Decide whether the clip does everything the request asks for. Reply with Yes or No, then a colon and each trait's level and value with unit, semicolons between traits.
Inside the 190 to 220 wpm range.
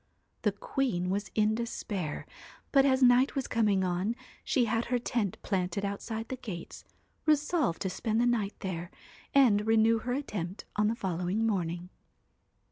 No: average, 155 wpm